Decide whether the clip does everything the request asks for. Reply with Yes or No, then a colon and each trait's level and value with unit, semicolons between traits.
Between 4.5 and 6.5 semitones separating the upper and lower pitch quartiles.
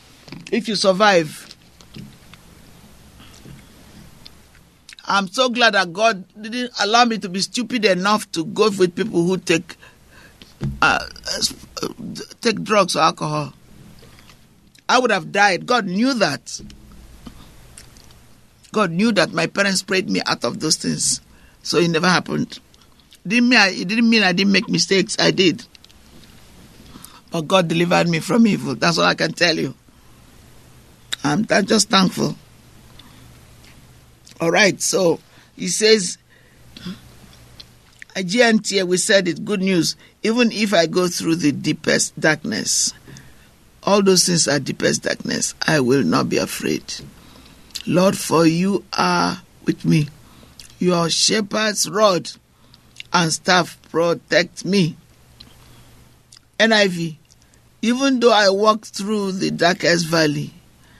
Yes: average, 4.8 semitones